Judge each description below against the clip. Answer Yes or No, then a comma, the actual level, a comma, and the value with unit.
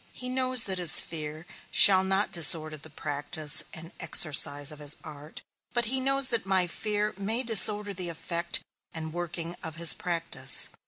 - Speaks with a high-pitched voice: No, medium, 175 Hz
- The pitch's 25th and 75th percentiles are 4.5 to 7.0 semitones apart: Yes, average, 4.9 semitones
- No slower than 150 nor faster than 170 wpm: Yes, average, 165 wpm